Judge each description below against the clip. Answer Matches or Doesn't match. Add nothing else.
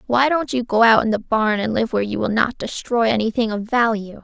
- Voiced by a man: Doesn't match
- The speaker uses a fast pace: Matches